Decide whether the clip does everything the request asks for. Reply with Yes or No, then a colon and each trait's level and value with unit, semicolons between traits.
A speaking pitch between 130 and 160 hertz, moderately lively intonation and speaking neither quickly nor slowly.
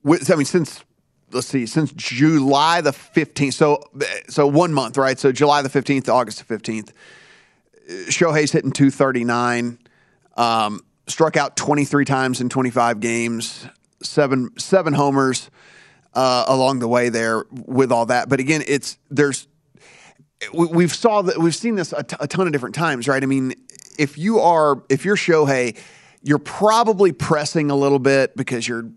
Yes: medium, 140 Hz; average, 3.8 semitones; average, 170 wpm